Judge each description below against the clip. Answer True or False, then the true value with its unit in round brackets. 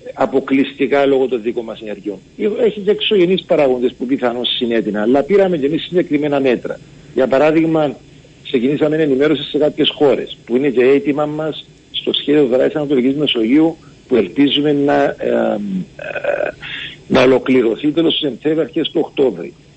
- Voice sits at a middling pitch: True (145 Hz)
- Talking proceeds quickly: False (150 wpm)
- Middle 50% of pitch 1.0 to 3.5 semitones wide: True (2.6 semitones)